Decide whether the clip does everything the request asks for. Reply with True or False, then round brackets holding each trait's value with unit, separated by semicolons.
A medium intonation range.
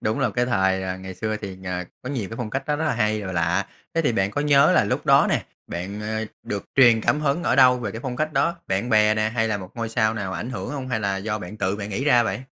True (4.3 semitones)